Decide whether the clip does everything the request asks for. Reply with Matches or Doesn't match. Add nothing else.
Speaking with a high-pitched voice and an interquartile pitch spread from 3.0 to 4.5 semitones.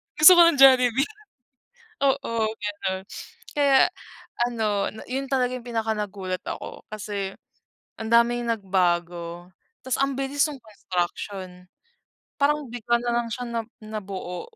Doesn't match